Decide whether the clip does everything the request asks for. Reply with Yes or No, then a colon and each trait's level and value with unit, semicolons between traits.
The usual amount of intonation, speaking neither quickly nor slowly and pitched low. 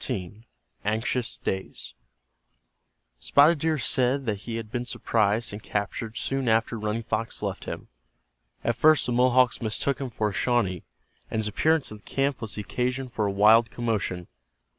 Yes: average, 3.0 semitones; average, 165 wpm; low, 115 Hz